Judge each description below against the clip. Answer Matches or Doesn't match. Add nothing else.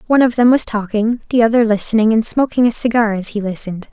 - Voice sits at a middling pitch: Doesn't match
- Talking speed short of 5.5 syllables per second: Doesn't match